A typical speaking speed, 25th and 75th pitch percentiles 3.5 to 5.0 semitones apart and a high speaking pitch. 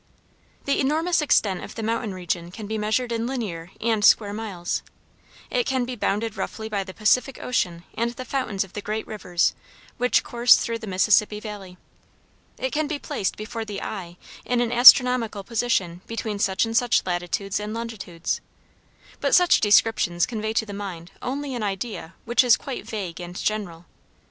Yes: average, 175 wpm; average, 3.8 semitones; high, 215 Hz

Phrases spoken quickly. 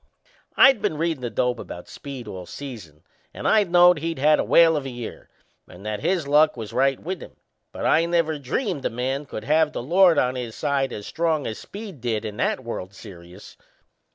Yes: fast, 210 wpm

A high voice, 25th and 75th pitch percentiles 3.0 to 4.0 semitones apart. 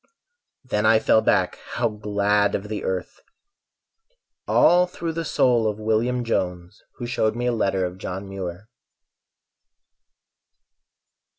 No: low, 105 Hz; average, 3.5 semitones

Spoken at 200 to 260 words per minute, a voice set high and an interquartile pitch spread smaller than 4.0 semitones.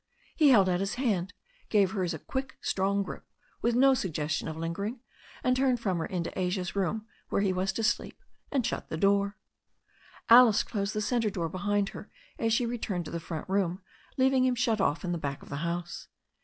No: fast, 205 wpm; high, 200 Hz; average, 4.8 semitones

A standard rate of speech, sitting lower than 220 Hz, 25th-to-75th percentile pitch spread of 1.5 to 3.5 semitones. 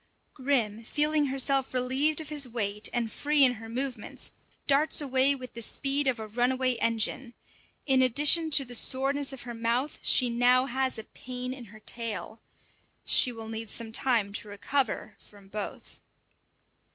No: average, 165 wpm; very high, 250 Hz; average, 3.1 semitones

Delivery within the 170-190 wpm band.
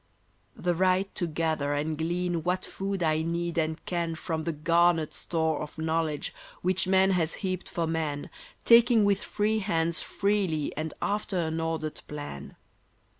No: average, 155 wpm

